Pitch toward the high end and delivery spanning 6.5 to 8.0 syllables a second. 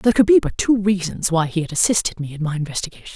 No: medium, 180 Hz; 7.2 syllables/s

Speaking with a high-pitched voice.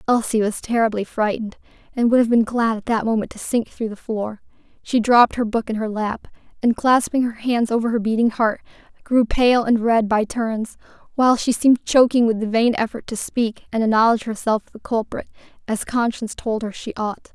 Yes: high, 225 Hz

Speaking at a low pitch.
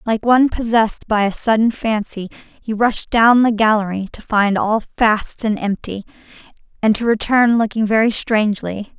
No: high, 220 Hz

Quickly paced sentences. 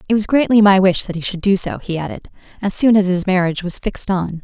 Yes: fast, 270 wpm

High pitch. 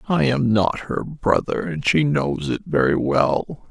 No: medium, 150 Hz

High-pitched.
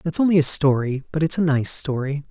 No: medium, 150 Hz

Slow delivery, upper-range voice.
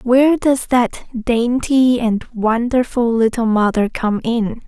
Yes: slow, 130 wpm; high, 235 Hz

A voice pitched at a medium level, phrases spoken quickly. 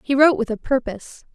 No: very high, 260 Hz; fast, 225 wpm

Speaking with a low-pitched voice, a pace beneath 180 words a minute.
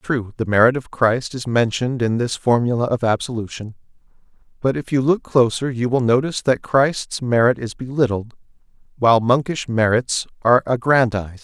Yes: low, 120 Hz; average, 155 wpm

